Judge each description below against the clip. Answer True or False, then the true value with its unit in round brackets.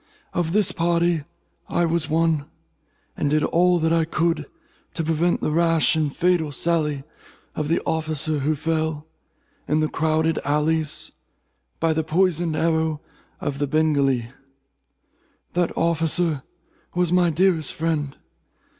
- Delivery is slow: True (130 wpm)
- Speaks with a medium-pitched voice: True (160 Hz)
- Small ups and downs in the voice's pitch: True (1.8 semitones)